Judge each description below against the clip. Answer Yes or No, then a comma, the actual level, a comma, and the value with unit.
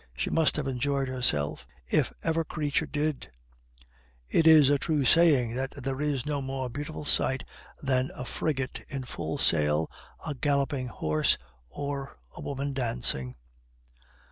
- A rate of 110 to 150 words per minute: Yes, average, 145 wpm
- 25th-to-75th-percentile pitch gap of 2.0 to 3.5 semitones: Yes, narrow, 2.6 semitones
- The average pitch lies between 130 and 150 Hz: Yes, low, 135 Hz